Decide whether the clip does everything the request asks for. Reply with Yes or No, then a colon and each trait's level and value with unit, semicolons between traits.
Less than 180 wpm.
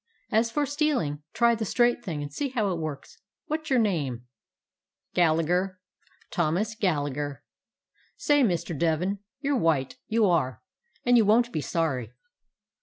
Yes: average, 150 wpm